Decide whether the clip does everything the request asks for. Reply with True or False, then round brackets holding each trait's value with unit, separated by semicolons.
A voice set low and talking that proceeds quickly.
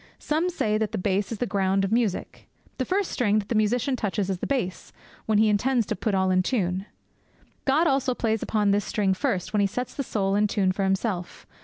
False (210 Hz; 225 wpm)